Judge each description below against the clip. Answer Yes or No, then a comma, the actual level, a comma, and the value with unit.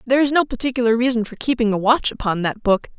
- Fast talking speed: Yes, fast, 240 wpm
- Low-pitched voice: No, high, 235 Hz